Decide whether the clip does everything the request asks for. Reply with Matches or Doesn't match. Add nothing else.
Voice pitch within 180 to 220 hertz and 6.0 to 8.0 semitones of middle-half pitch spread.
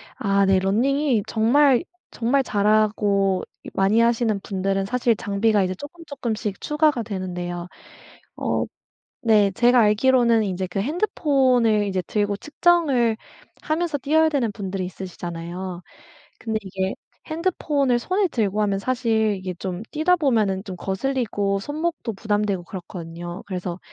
Doesn't match